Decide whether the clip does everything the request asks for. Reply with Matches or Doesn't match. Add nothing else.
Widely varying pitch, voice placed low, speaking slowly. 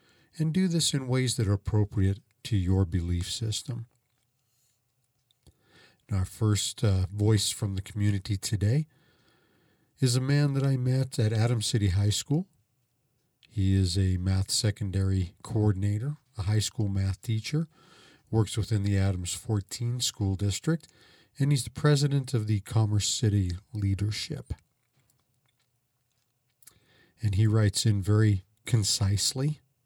Doesn't match